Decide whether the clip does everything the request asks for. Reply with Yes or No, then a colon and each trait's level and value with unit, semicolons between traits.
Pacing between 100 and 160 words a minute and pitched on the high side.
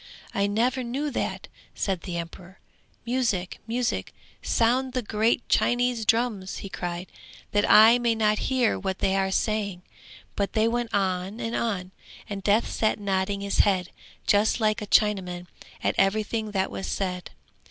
Yes: average, 155 wpm; high, 210 Hz